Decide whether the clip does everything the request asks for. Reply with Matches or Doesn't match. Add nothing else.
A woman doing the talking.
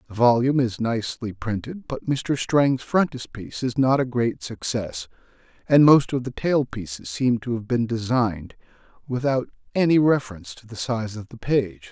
Doesn't match